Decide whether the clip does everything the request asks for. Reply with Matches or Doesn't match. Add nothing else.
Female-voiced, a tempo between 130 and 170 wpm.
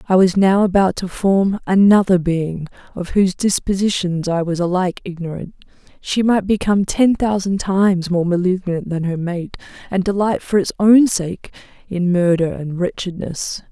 Matches